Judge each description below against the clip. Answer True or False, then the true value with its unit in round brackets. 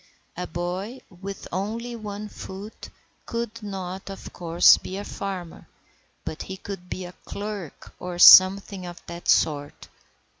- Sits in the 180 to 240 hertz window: True (190 Hz)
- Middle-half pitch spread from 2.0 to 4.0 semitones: True (2.5 semitones)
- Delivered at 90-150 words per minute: True (140 wpm)